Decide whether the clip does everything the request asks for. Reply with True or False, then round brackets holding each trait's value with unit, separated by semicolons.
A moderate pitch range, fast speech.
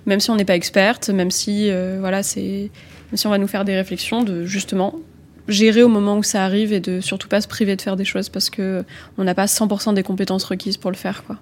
False (1.5 semitones; 265 wpm)